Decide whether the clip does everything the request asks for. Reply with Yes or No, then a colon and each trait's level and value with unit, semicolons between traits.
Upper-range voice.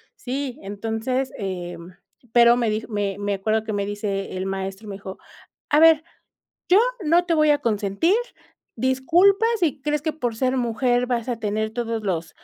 Yes: high, 230 Hz